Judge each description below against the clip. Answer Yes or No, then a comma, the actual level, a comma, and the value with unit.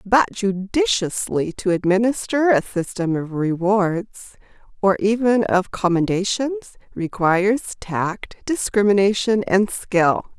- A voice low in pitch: No, high, 200 Hz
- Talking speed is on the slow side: Yes, slow, 100 wpm